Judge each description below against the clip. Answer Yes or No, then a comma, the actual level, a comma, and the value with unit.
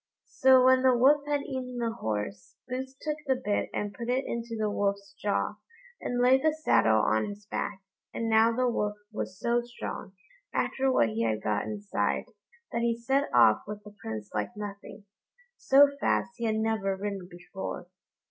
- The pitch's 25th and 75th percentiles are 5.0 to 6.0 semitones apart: No, average, 4.6 semitones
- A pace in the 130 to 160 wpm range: No, average, 180 wpm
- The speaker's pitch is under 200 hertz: No, high, 220 Hz